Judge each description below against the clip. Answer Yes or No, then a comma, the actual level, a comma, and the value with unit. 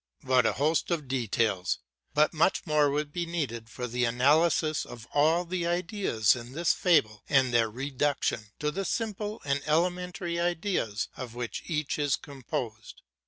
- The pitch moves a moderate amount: No, wide, 5.8 semitones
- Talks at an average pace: Yes, average, 160 wpm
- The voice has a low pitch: No, medium, 145 Hz